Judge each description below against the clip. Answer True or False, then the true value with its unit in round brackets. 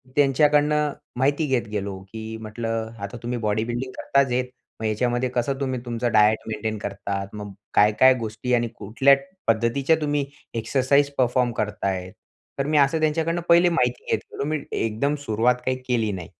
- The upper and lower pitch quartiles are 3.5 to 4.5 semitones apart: True (4.2 semitones)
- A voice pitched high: False (120 Hz)